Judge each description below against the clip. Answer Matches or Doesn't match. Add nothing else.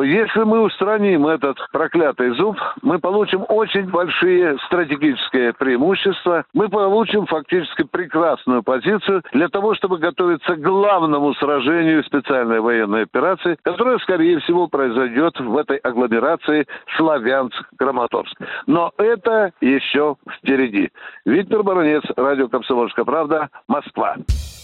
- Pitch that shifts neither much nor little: Doesn't match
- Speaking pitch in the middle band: Matches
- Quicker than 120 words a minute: Doesn't match